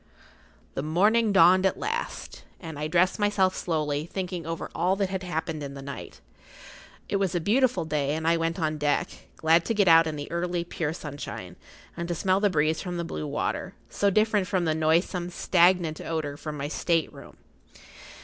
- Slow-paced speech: No, average, 195 wpm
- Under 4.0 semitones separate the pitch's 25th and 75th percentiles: Yes, average, 3.2 semitones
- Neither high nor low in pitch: Yes, medium, 170 Hz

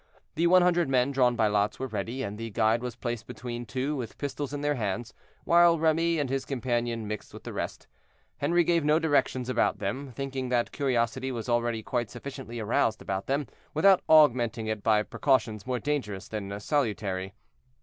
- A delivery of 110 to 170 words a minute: No, average, 185 wpm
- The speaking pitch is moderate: No, low, 125 Hz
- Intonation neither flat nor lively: Yes, average, 4.2 semitones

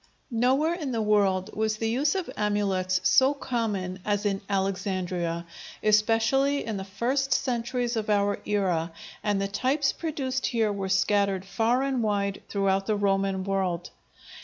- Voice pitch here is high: Yes, high, 205 Hz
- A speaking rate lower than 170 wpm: Yes, average, 150 wpm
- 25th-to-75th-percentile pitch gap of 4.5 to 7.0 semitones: No, average, 3.8 semitones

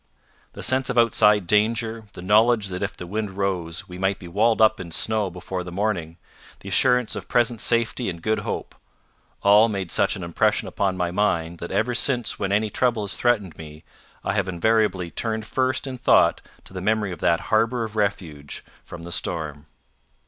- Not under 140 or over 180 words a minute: No, average, 190 wpm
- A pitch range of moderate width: Yes, average, 3.9 semitones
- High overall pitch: No, low, 105 Hz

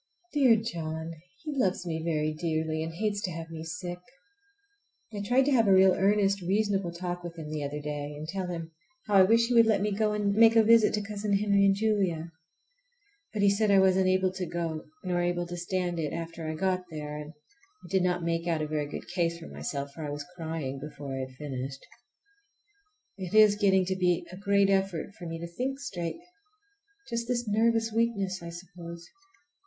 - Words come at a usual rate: No, fast, 210 wpm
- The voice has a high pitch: No, medium, 180 Hz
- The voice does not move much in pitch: No, average, 3.8 semitones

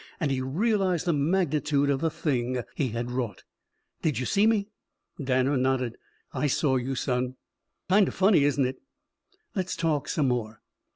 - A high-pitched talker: No, medium, 140 Hz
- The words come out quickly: No, average, 165 wpm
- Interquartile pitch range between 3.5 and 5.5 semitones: Yes, average, 4.7 semitones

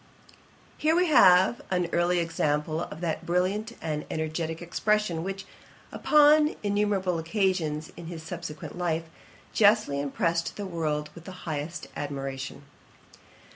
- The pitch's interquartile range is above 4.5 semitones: No, average, 3.6 semitones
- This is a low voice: No, medium, 170 Hz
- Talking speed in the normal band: No, slow, 125 wpm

